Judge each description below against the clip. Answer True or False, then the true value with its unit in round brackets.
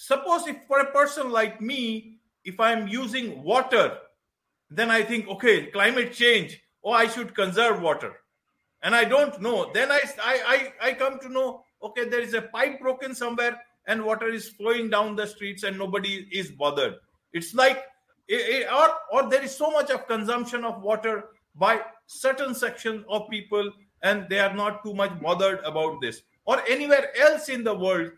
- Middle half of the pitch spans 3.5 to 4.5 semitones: True (4.1 semitones)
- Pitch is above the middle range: True (230 Hz)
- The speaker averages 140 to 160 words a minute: False (180 wpm)